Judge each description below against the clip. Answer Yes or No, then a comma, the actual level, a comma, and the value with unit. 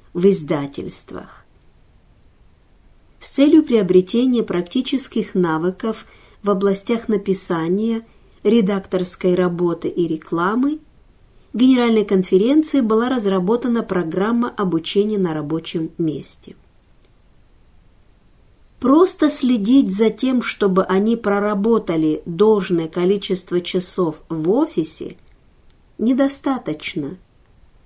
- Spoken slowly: Yes, slow, 80 wpm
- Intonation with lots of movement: No, average, 5.0 semitones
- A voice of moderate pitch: No, high, 200 Hz